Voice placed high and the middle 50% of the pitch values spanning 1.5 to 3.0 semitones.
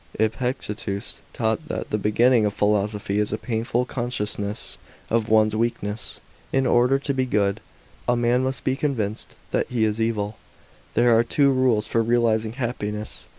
No: low, 115 Hz; narrow, 2.6 semitones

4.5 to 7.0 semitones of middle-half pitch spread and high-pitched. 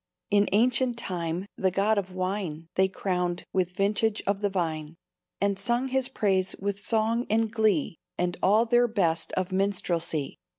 No: average, 3.4 semitones; high, 195 Hz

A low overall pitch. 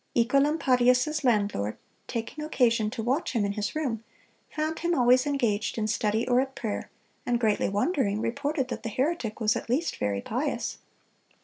No: high, 245 Hz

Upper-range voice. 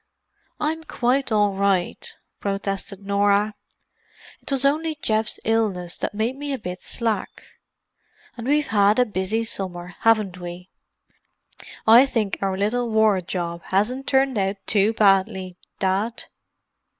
Yes: high, 210 Hz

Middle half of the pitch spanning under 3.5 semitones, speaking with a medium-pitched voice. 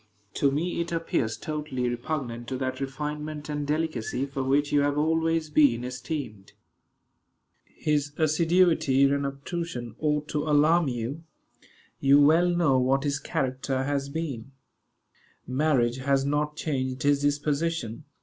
Yes: average, 2.8 semitones; medium, 145 Hz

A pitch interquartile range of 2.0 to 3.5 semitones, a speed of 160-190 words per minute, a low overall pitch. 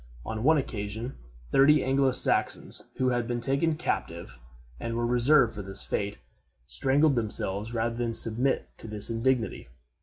No: average, 3.2 semitones; average, 150 wpm; low, 120 Hz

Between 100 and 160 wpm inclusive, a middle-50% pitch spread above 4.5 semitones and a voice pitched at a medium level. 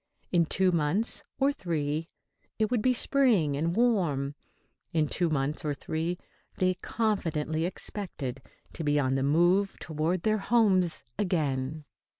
Yes: average, 140 wpm; average, 5.1 semitones; medium, 170 Hz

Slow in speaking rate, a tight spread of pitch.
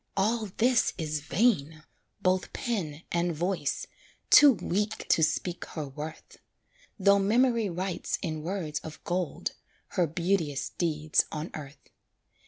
No: slow, 125 wpm; average, 4.4 semitones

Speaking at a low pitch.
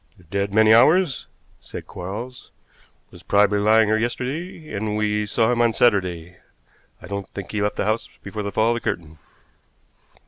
Yes: low, 105 Hz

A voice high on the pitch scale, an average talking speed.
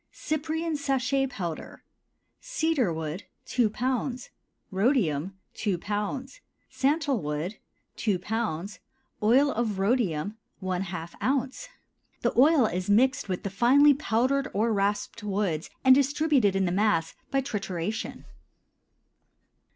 No: high, 220 Hz; slow, 110 wpm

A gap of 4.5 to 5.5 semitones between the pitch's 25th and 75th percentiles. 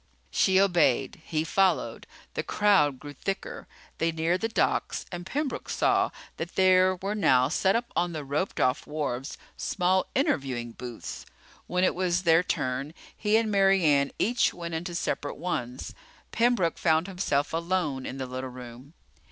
Yes: average, 5.2 semitones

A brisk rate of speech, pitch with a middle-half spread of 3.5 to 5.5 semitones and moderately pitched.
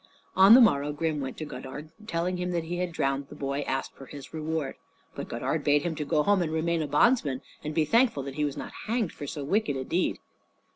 Yes: fast, 235 wpm; average, 3.9 semitones; medium, 155 Hz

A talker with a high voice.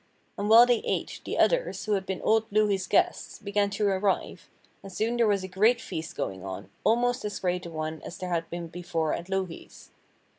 Yes: high, 195 Hz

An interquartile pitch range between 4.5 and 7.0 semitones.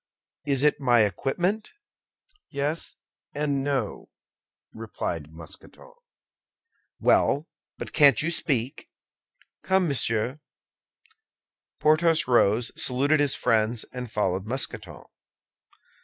Yes: average, 5.1 semitones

